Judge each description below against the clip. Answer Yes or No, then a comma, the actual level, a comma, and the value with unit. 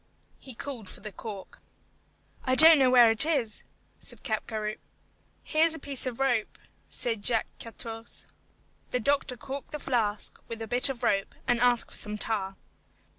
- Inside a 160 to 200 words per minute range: Yes, average, 170 wpm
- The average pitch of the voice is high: Yes, high, 240 Hz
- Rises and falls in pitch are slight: No, average, 3.7 semitones